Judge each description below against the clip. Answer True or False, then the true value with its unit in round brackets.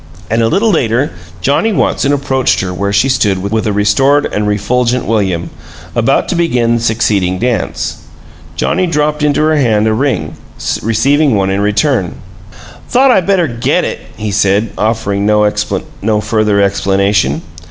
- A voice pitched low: True (110 Hz)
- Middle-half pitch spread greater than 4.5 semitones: True (5.3 semitones)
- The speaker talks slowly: False (155 wpm)